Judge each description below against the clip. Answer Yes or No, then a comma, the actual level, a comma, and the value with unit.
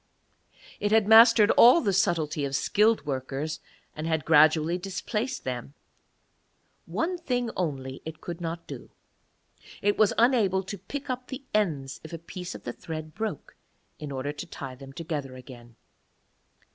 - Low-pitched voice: No, medium, 165 Hz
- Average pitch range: No, wide, 6.7 semitones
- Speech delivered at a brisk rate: No, average, 155 wpm